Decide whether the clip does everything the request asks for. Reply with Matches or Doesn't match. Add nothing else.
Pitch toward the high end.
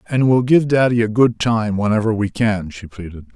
Doesn't match